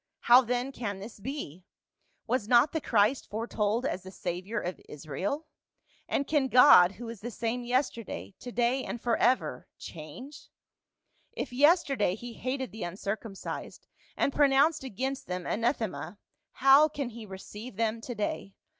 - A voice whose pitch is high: Yes, high, 235 Hz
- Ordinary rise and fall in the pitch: Yes, average, 4.6 semitones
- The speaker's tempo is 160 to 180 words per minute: No, average, 145 wpm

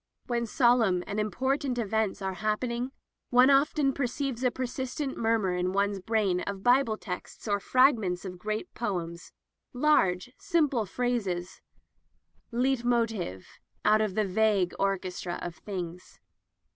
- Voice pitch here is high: Yes, high, 220 Hz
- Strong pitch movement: No, average, 4.7 semitones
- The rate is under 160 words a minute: Yes, slow, 135 wpm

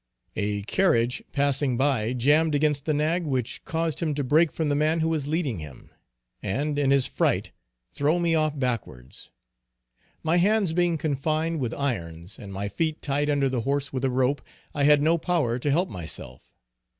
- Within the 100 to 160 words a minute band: No, average, 180 wpm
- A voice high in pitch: No, medium, 145 Hz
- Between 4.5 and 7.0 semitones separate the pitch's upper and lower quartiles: No, average, 4.1 semitones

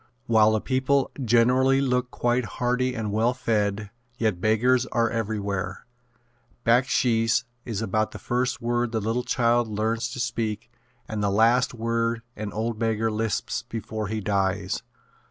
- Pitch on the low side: Yes, low, 115 Hz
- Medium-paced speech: Yes, average, 145 wpm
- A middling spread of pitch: No, narrow, 2.2 semitones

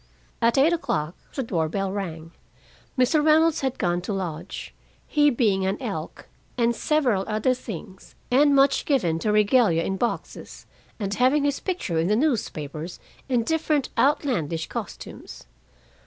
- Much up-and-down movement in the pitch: Yes, wide, 7.3 semitones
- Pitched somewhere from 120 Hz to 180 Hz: No, high, 225 Hz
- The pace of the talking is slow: No, average, 145 wpm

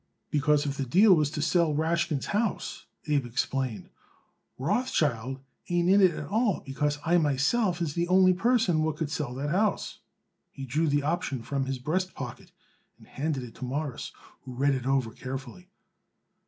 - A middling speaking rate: Yes, average, 170 wpm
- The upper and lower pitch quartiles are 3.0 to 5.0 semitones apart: Yes, average, 4.6 semitones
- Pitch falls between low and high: Yes, medium, 150 Hz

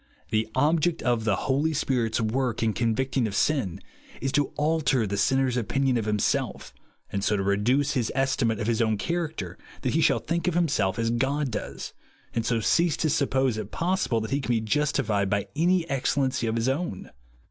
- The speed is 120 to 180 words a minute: No, average, 190 wpm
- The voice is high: No, low, 125 Hz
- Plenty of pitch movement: No, average, 4.8 semitones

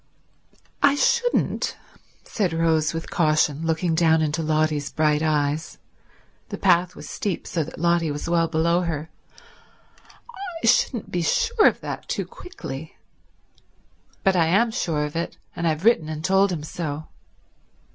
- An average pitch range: Yes, average, 3.1 semitones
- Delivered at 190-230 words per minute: No, average, 140 wpm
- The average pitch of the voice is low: No, medium, 165 Hz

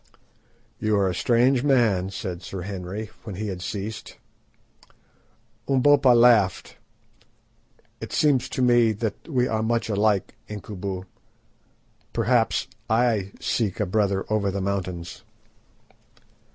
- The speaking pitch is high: No, low, 105 Hz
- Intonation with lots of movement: No, average, 3.5 semitones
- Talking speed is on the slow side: Yes, slow, 115 wpm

